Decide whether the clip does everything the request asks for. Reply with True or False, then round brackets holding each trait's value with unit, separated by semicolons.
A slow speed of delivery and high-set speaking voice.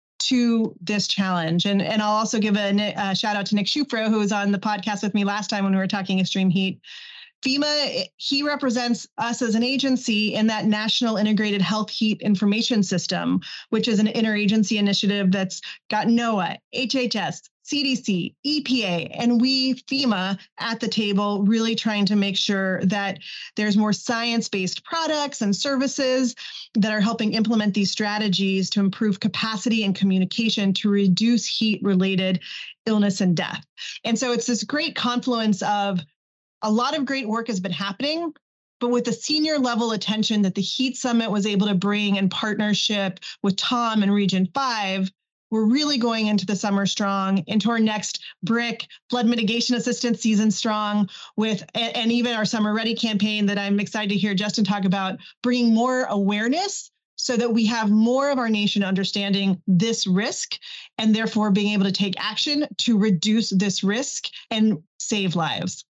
False (170 wpm; 215 Hz)